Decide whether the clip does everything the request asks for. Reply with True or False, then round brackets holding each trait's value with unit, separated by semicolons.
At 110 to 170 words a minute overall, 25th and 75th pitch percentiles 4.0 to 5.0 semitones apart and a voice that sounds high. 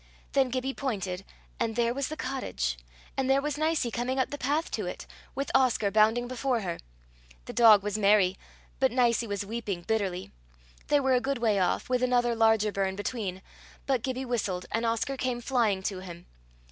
False (185 wpm; 4.4 semitones; 235 Hz)